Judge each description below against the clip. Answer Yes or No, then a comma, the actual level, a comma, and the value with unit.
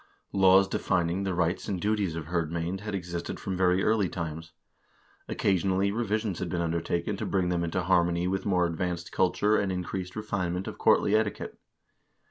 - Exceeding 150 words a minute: Yes, average, 170 wpm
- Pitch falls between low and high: No, very low, 90 Hz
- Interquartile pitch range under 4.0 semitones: Yes, narrow, 2.4 semitones